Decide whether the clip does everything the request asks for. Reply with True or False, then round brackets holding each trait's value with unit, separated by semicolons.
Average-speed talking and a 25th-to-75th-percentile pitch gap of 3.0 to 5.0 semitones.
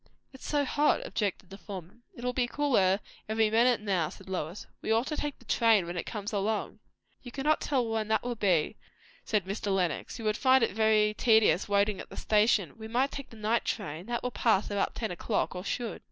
False (225 wpm; 3.4 semitones)